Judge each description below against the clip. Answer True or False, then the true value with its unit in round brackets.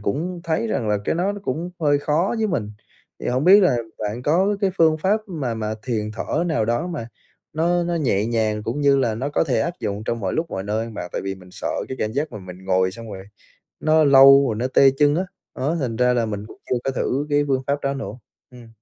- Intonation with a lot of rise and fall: True (6.5 semitones)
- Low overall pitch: True (130 Hz)